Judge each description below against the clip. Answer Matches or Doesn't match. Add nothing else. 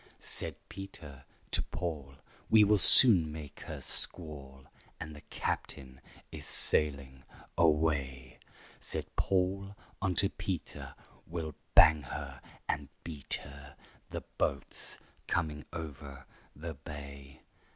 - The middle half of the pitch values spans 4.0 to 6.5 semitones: Doesn't match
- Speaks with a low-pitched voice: Matches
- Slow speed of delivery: Matches